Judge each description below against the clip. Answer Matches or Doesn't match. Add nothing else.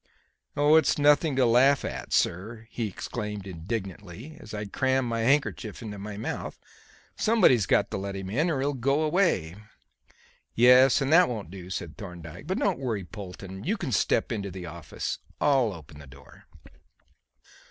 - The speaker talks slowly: Doesn't match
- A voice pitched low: Matches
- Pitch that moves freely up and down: Matches